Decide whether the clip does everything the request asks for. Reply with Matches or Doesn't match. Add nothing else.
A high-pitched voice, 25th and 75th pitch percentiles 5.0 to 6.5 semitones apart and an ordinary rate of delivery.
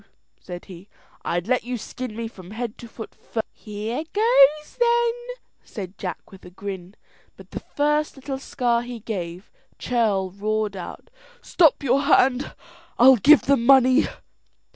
Matches